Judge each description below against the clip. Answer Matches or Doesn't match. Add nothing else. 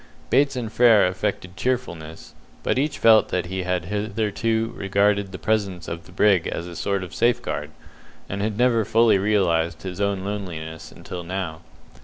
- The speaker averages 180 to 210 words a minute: Doesn't match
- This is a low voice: Matches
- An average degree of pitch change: Matches